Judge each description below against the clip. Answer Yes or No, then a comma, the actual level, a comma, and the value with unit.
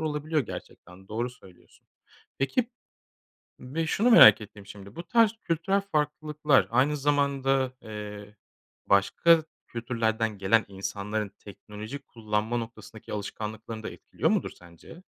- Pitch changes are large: Yes, wide, 6.0 semitones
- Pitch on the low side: Yes, low, 115 Hz